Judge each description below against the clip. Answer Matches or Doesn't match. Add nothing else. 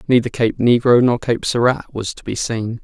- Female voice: Doesn't match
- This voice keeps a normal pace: Doesn't match